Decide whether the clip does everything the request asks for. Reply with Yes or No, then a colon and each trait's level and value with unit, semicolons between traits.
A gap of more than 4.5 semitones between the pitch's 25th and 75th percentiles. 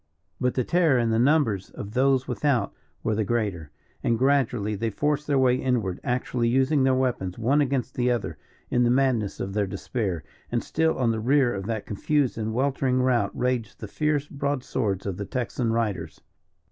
No: average, 3.8 semitones